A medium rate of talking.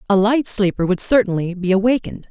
Yes: average, 180 wpm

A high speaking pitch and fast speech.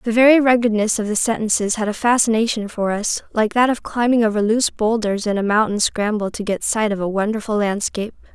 Yes: high, 220 Hz; fast, 210 wpm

